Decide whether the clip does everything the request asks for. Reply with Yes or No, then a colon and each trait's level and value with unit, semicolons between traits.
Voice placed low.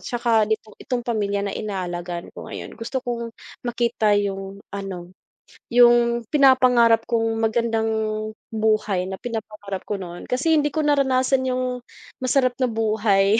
No: high, 225 Hz